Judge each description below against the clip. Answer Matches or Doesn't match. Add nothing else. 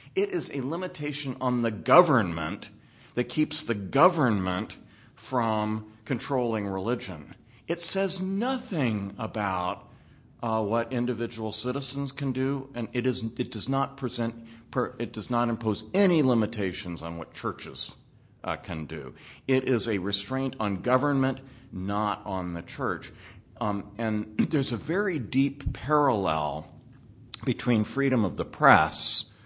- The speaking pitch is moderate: Doesn't match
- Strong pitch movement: Doesn't match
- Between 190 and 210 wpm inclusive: Doesn't match